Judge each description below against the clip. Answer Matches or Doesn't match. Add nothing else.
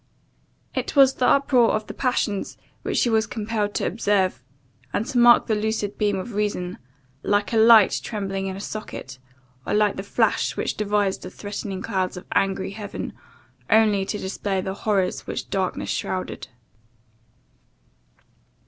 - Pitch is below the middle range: Doesn't match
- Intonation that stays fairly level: Matches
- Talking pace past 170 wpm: Doesn't match